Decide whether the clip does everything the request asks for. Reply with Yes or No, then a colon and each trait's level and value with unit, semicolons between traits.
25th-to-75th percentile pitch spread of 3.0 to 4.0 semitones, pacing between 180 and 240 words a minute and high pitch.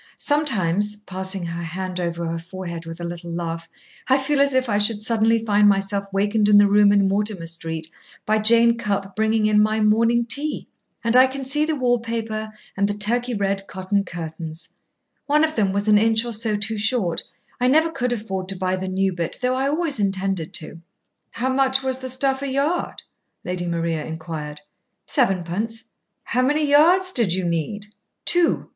No: average, 5.0 semitones; average, 185 wpm; high, 210 Hz